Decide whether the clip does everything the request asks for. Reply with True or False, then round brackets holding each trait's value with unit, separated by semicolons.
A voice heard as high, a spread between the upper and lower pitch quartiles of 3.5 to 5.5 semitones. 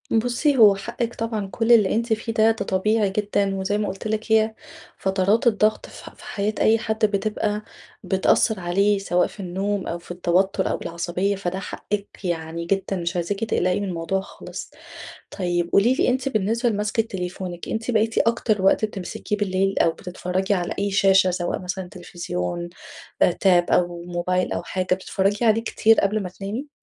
False (195 Hz; 3.0 semitones)